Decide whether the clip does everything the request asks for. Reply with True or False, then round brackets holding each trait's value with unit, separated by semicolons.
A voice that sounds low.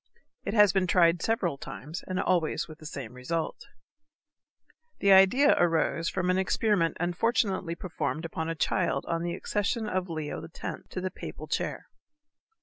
False (175 Hz)